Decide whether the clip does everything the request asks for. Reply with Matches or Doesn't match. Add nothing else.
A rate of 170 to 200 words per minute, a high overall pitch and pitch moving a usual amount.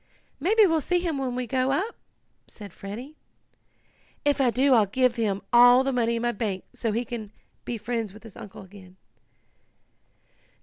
Matches